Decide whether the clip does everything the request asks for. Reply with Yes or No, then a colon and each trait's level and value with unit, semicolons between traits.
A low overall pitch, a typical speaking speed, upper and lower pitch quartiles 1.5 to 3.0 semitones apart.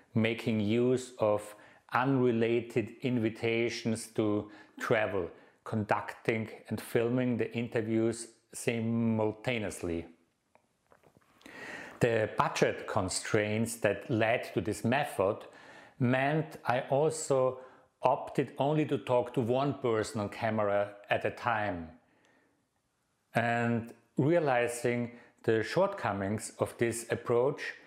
No: low, 115 Hz; slow, 95 wpm; narrow, 2.4 semitones